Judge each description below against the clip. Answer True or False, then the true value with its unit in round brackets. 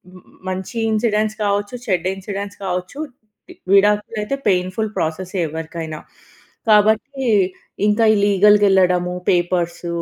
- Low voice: False (195 Hz)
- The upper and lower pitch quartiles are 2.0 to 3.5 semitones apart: True (2.7 semitones)